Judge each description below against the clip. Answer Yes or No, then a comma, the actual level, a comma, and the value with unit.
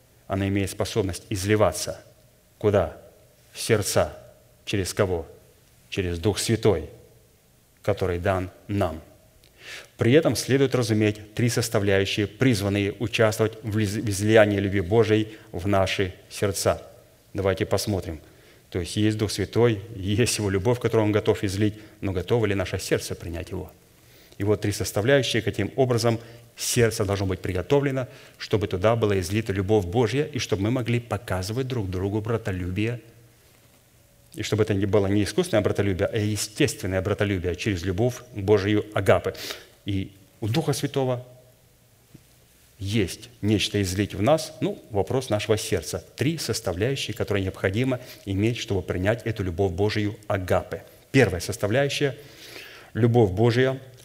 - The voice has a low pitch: Yes, low, 105 Hz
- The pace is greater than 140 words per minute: No, average, 130 wpm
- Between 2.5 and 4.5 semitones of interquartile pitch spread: Yes, average, 3.0 semitones